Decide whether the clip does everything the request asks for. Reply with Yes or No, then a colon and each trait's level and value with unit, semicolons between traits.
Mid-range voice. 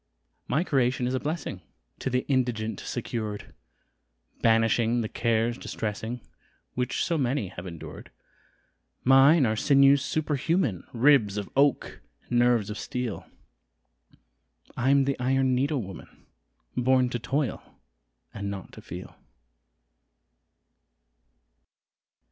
No: low, 125 Hz